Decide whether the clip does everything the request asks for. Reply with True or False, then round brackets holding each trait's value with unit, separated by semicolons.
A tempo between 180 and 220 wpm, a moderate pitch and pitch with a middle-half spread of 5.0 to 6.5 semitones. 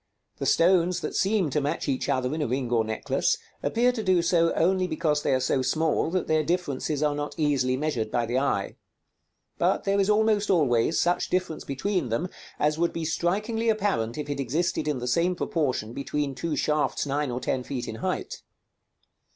True (195 wpm; 155 Hz; 5.4 semitones)